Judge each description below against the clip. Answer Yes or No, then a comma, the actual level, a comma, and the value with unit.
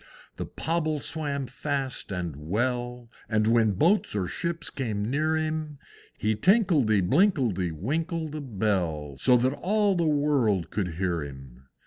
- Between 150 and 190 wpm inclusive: No, average, 140 wpm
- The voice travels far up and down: Yes, wide, 8.3 semitones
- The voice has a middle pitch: No, low, 125 Hz